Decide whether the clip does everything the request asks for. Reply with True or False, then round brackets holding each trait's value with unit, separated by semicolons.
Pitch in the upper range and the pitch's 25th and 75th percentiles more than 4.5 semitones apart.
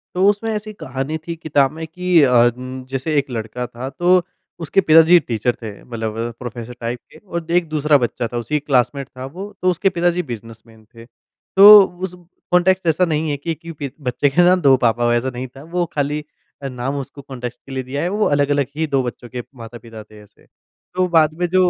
False (140 Hz; 5.5 semitones)